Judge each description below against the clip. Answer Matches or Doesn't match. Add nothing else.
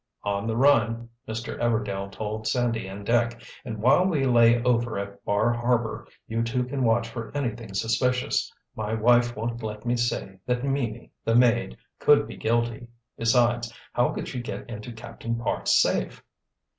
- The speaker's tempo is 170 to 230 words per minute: Doesn't match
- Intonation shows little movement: Matches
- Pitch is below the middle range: Matches